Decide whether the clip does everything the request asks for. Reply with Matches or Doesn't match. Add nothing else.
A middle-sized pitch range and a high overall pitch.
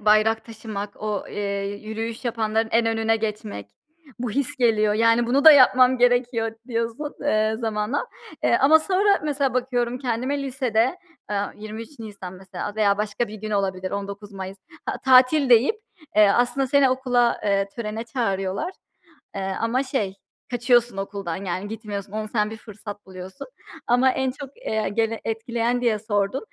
Matches